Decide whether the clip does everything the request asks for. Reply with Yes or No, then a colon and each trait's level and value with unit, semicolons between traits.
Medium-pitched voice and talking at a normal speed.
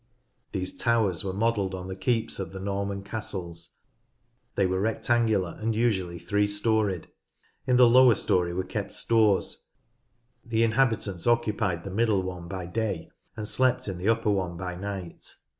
No: low, 100 Hz; average, 160 wpm